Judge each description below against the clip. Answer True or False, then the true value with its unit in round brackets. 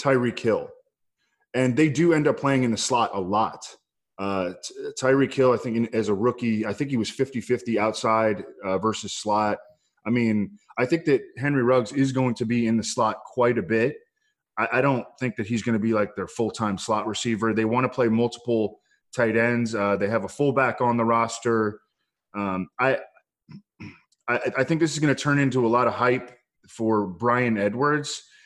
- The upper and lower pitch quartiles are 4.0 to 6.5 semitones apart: False (3.4 semitones)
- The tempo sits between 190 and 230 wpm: True (205 wpm)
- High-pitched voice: False (120 Hz)